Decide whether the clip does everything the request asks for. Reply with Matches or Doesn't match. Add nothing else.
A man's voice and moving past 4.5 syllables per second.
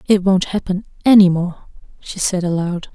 Doesn't match